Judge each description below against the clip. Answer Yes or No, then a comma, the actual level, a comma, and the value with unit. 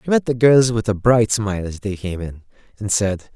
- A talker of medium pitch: No, low, 110 Hz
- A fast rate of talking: Yes, fast, 250 wpm